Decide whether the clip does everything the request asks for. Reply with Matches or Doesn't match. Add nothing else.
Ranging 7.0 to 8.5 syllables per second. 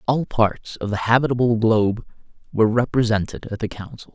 Doesn't match